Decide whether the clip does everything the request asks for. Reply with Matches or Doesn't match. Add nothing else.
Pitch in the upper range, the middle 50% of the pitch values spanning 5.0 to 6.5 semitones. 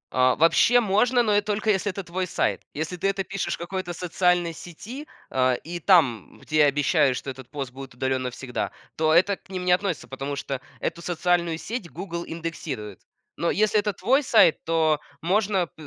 Doesn't match